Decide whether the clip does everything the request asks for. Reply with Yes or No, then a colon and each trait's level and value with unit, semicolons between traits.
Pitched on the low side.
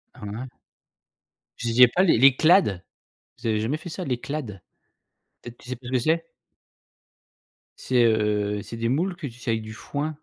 Yes: low, 125 Hz